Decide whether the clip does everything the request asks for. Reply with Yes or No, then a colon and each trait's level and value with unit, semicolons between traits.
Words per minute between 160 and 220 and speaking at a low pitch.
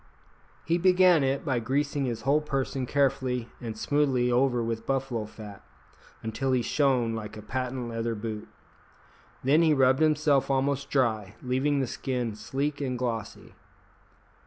No: average, 145 wpm; low, 130 Hz